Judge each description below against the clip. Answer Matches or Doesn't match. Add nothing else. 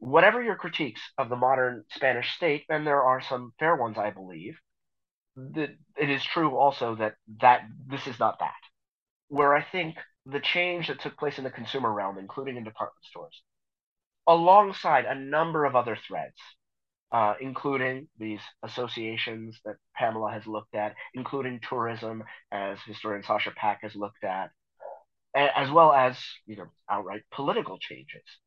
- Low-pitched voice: Matches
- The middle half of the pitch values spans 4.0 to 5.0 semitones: Matches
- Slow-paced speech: Doesn't match